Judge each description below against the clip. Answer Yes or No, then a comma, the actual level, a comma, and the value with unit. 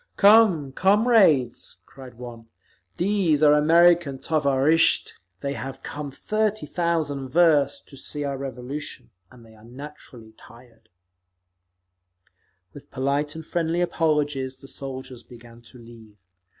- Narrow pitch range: No, average, 4.3 semitones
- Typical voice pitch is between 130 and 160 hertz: Yes, medium, 140 Hz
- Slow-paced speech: Yes, slow, 120 wpm